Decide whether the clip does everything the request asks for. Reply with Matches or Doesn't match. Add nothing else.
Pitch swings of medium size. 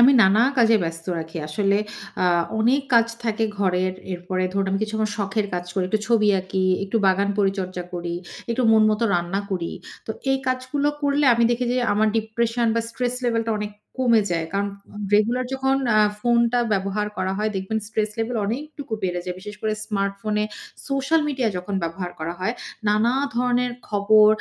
Matches